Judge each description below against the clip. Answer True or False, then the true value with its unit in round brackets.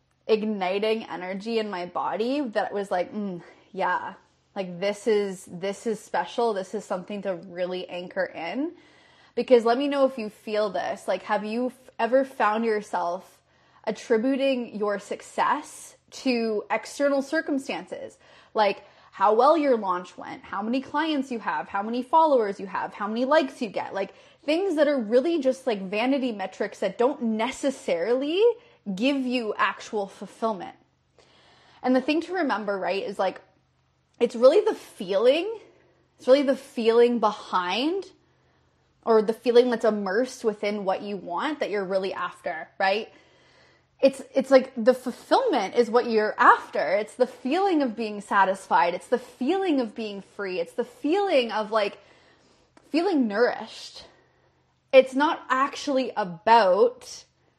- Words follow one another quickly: False (150 wpm)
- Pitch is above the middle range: True (235 Hz)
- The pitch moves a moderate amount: True (5.0 semitones)